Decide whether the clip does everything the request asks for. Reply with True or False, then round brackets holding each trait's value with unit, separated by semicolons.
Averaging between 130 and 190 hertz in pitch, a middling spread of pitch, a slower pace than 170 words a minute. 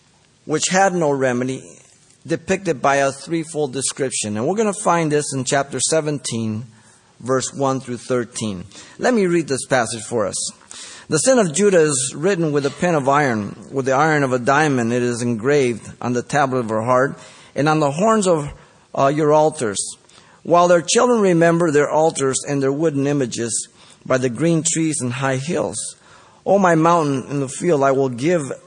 False (140 Hz; 4.2 semitones; 190 wpm)